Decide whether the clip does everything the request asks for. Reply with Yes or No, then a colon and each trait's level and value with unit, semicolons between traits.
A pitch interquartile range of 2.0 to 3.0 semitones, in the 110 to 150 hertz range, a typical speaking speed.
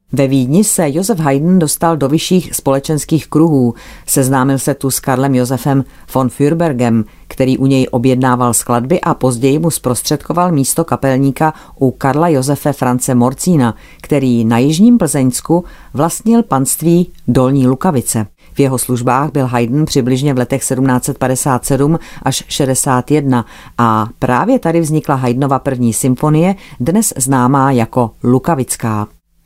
No: average, 3.6 semitones; low, 135 Hz; average, 130 wpm